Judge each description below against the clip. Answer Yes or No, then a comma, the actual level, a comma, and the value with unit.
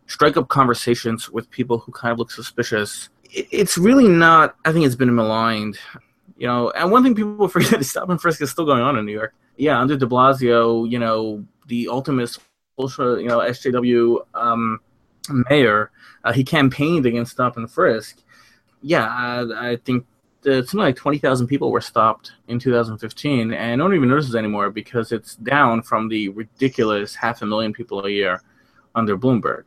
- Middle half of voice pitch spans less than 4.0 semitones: Yes, average, 3.4 semitones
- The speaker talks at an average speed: Yes, average, 185 wpm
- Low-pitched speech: Yes, low, 120 Hz